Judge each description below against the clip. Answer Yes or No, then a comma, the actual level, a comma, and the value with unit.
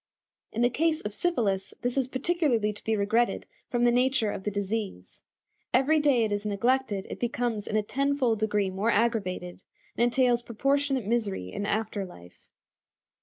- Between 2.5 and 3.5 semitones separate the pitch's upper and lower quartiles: No, average, 3.9 semitones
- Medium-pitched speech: No, high, 230 Hz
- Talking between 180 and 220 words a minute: No, average, 170 wpm